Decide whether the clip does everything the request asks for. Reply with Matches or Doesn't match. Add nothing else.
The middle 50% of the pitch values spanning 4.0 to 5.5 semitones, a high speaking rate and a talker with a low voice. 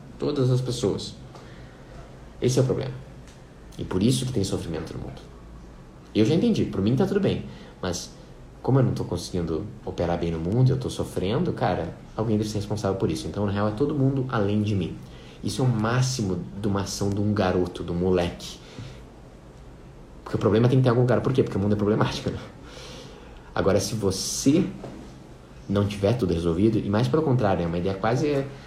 Matches